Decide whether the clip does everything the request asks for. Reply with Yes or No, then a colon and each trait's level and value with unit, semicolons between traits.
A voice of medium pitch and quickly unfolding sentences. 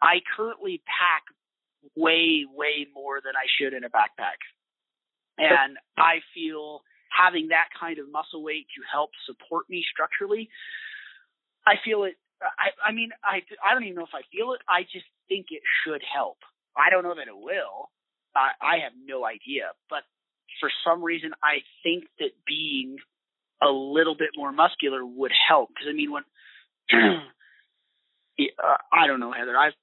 No: medium, 170 Hz; average, 165 wpm